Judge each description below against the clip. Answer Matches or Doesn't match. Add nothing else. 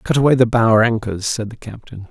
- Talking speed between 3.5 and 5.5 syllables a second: Doesn't match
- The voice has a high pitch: Doesn't match